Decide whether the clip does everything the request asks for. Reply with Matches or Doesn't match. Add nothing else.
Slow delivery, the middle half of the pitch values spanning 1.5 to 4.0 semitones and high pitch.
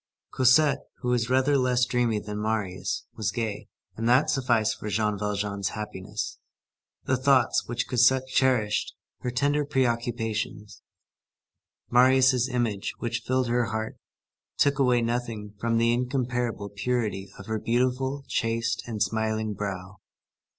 Doesn't match